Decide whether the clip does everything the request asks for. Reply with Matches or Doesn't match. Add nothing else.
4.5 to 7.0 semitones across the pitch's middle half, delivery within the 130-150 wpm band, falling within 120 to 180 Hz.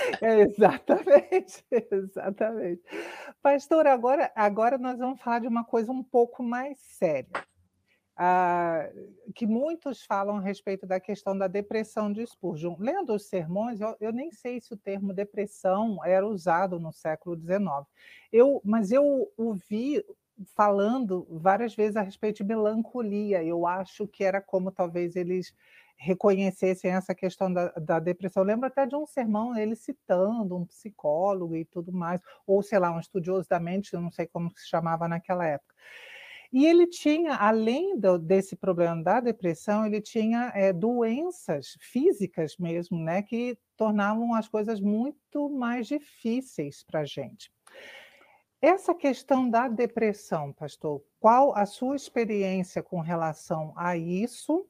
Doesn't match